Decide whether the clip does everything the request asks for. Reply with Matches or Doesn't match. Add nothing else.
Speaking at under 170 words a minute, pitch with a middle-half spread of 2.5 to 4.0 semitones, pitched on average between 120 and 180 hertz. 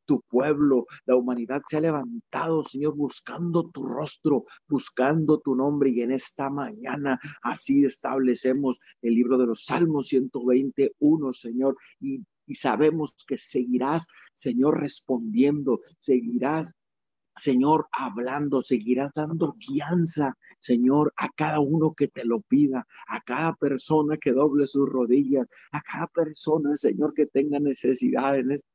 Matches